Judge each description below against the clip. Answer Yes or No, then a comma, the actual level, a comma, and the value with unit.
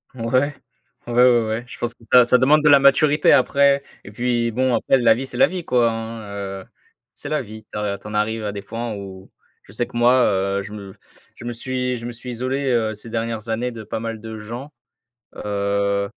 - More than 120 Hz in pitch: No, low, 115 Hz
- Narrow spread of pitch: No, average, 3.0 semitones